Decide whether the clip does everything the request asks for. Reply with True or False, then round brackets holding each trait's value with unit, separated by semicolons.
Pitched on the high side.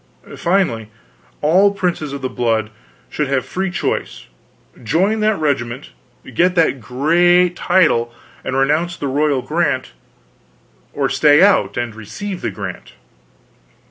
False (150 Hz)